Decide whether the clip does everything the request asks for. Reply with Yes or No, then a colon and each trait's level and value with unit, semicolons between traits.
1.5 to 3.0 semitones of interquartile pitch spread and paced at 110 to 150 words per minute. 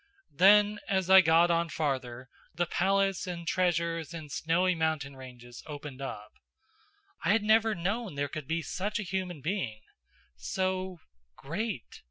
No: average, 4.8 semitones; average, 145 wpm